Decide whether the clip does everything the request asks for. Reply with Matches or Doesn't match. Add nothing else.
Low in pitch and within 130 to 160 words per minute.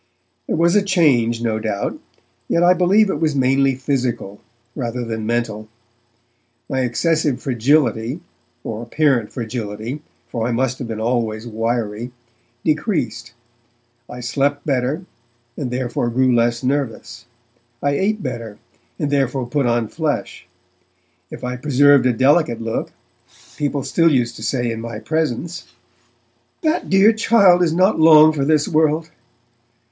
Matches